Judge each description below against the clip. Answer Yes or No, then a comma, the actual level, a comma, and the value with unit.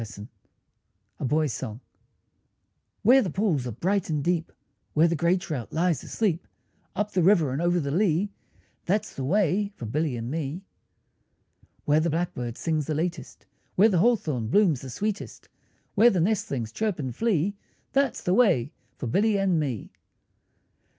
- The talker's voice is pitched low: No, medium, 165 Hz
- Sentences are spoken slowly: No, average, 165 wpm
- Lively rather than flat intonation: Yes, wide, 6.2 semitones